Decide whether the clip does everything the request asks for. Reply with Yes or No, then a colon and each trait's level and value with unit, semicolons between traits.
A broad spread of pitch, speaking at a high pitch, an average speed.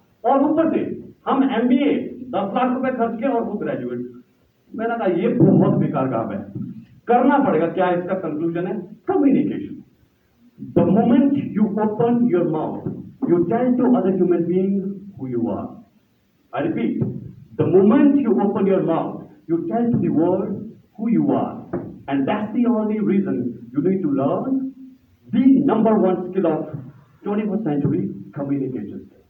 Yes: wide, 6.4 semitones; high, 205 Hz; average, 145 wpm